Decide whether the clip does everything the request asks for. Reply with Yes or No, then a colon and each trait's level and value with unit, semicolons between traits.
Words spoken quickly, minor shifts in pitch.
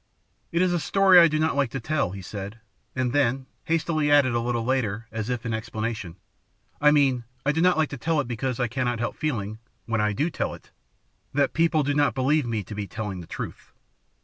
No: fast, 225 wpm; average, 5.0 semitones